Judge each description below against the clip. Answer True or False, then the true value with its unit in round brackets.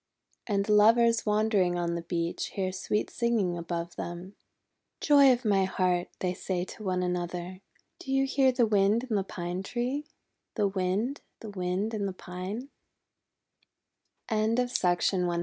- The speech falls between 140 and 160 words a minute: True (145 wpm)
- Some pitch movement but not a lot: True (4.0 semitones)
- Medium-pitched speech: False (195 Hz)